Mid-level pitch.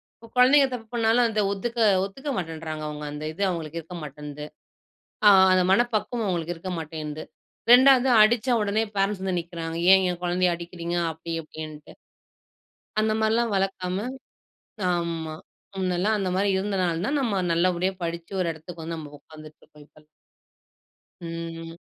Yes: medium, 175 Hz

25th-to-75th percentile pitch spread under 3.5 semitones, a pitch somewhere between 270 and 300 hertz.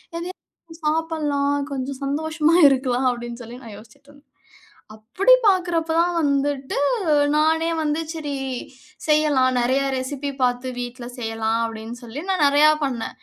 No: average, 4.2 semitones; very high, 280 Hz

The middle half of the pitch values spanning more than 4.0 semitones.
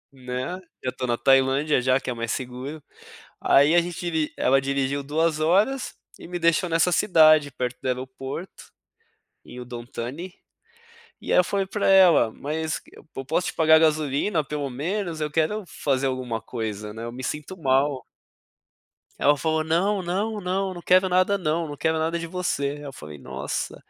Yes: average, 4.9 semitones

